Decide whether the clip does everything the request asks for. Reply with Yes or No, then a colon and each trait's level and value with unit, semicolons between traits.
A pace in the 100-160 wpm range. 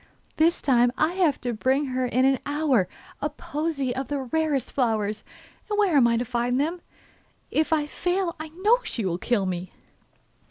No: average, 185 wpm